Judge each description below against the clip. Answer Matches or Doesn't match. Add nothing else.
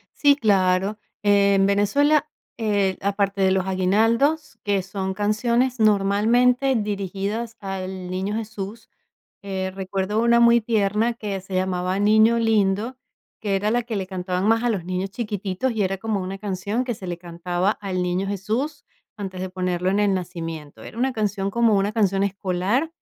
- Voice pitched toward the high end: Matches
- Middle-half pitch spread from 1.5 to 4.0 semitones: Matches